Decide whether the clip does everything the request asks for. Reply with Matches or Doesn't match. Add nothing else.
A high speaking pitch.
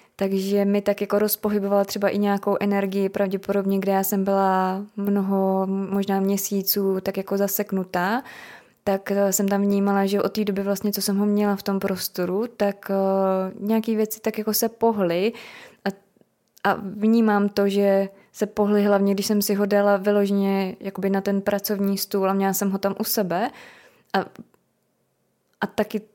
Matches